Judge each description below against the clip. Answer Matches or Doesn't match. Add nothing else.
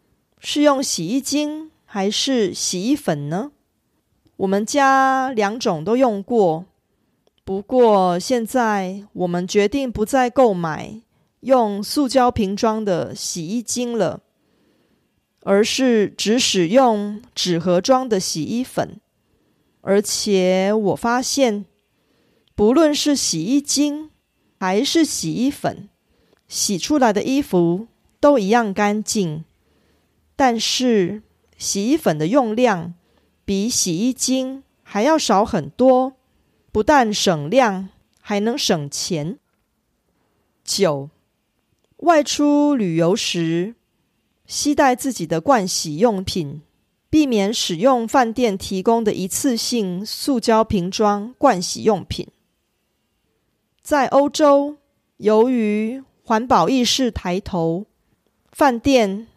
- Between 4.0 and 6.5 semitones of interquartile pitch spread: Matches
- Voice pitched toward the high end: Matches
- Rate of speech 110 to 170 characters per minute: Matches